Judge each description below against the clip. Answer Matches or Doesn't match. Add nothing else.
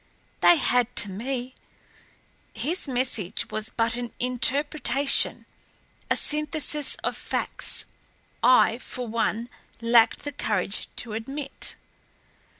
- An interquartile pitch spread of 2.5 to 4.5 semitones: Matches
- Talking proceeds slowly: Matches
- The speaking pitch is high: Matches